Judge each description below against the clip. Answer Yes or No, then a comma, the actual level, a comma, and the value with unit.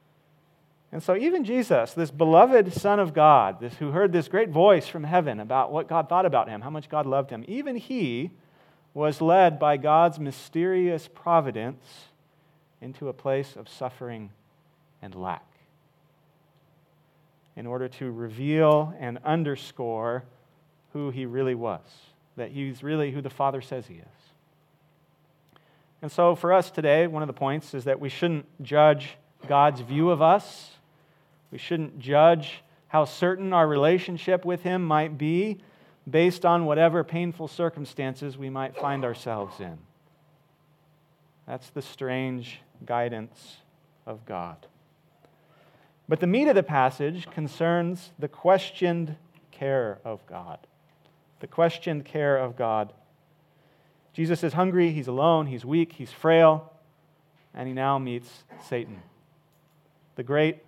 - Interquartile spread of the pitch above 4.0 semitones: No, average, 3.3 semitones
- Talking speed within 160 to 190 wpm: No, average, 140 wpm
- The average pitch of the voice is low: No, medium, 155 Hz